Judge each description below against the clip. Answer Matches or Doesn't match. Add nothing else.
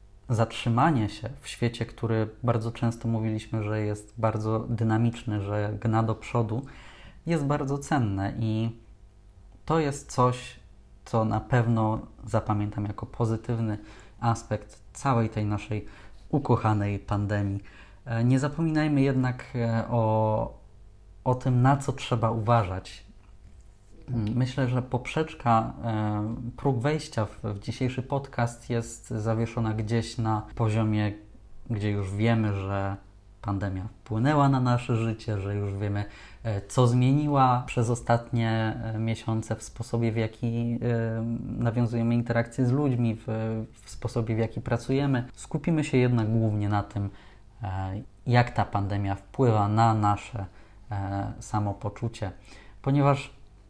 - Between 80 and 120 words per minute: Matches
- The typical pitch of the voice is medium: Doesn't match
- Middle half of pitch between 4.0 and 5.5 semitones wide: Doesn't match